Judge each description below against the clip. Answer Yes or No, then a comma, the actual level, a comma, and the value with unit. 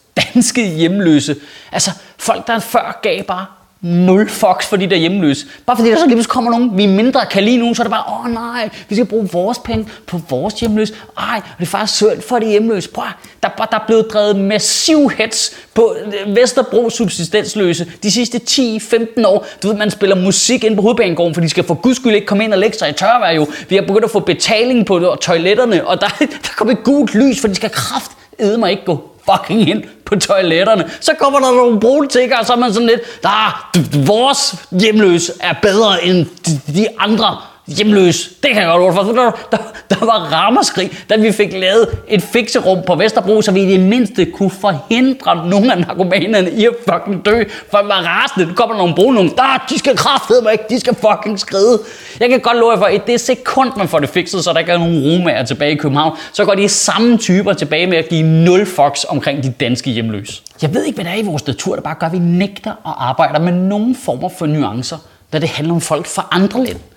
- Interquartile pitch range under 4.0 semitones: No, average, 4.7 semitones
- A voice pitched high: Yes, high, 205 Hz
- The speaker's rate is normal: No, fast, 230 wpm